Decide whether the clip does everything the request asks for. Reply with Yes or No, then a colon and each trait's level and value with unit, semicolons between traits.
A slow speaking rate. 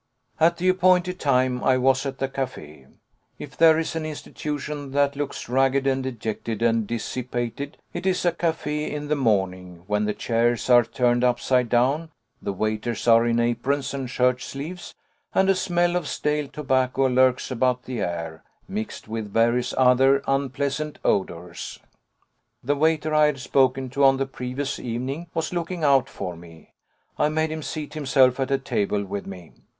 No: average, 170 wpm